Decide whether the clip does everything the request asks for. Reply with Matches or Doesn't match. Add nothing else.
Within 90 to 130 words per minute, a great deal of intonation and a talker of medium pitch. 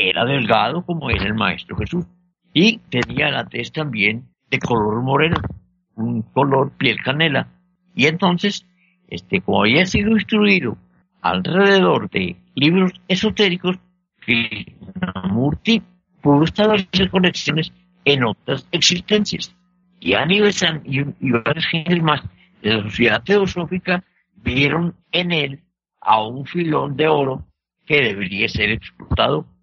Matches